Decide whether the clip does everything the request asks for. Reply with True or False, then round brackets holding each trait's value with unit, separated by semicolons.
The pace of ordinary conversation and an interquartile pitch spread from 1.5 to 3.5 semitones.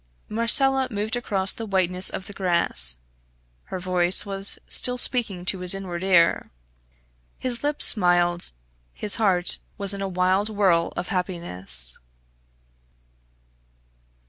False (120 wpm; 2.9 semitones)